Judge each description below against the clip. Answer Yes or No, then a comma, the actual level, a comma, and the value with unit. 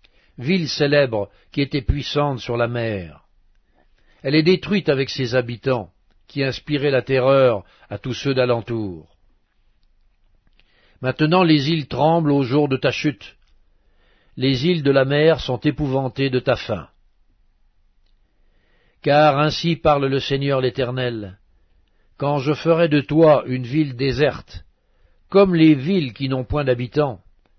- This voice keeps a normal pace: No, slow, 135 wpm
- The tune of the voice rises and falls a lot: Yes, wide, 6.3 semitones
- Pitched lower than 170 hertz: Yes, low, 135 Hz